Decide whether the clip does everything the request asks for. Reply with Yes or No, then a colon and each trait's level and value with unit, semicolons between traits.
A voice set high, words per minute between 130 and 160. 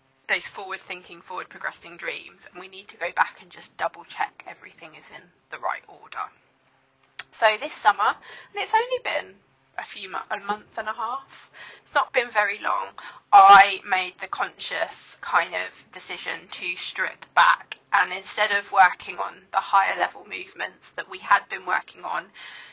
No: high, 205 Hz; average, 175 wpm